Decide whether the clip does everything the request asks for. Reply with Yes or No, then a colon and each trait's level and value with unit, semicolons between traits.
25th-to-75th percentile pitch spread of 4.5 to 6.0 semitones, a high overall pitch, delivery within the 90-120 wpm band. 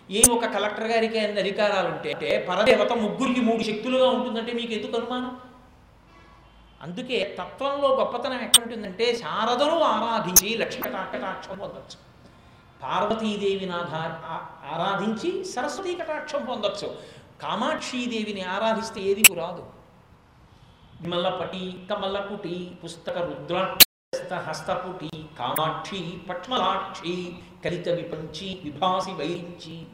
No: average, 5.1 semitones; high, 200 Hz; average, 80 wpm